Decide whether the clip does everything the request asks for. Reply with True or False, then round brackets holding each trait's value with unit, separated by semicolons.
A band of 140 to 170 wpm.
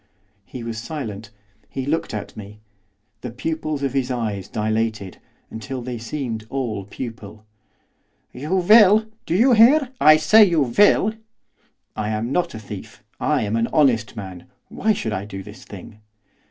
True (155 wpm)